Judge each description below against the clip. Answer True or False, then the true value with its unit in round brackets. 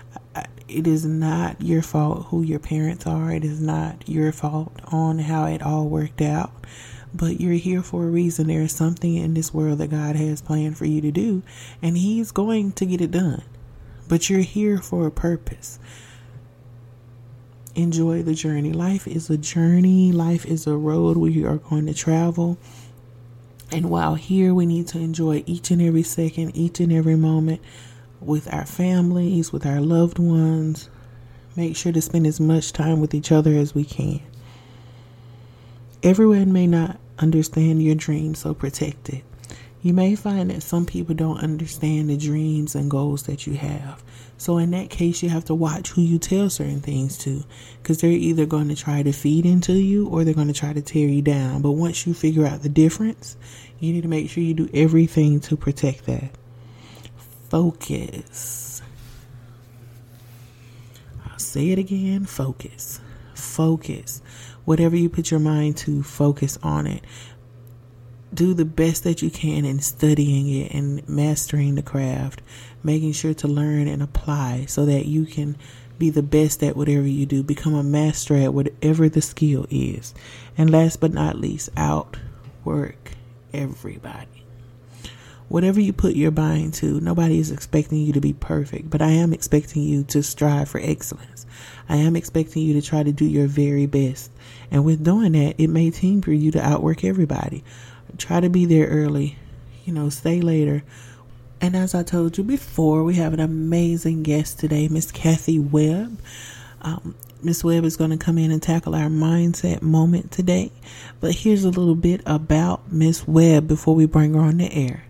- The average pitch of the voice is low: False (155 Hz)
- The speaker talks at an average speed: True (180 wpm)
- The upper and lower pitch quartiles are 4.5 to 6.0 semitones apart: False (4.1 semitones)